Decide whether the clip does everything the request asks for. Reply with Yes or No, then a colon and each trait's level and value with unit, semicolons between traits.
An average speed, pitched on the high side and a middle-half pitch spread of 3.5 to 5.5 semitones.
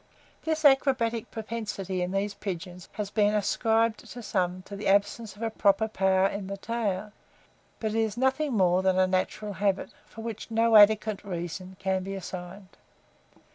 No: average, 165 wpm; high, 205 Hz; average, 3.0 semitones